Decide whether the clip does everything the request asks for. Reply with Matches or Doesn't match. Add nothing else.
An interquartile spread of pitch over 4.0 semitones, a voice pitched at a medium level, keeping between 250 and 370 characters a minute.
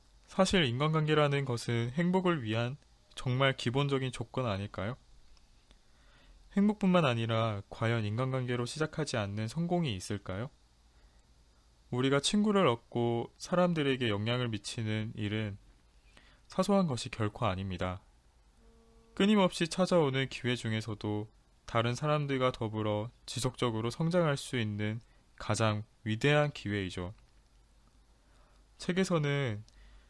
Doesn't match